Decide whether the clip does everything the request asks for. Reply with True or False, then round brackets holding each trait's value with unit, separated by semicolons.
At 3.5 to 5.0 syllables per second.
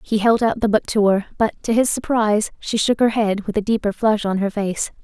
False (5.3 syllables/s)